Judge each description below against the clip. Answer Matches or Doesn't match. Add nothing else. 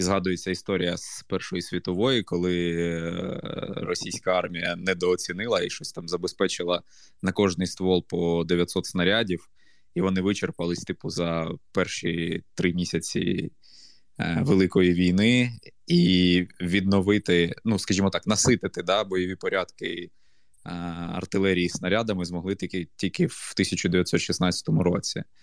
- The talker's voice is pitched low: Matches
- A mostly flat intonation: Matches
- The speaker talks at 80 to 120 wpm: Matches